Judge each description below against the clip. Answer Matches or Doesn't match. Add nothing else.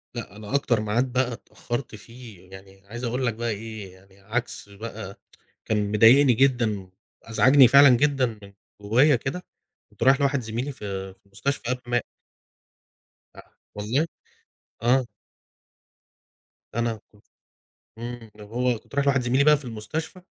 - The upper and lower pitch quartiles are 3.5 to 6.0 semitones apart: Matches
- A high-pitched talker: Doesn't match